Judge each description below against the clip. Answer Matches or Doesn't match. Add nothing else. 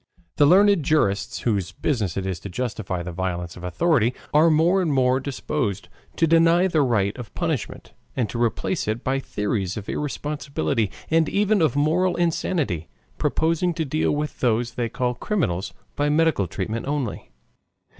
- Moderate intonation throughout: Doesn't match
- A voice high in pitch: Doesn't match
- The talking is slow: Doesn't match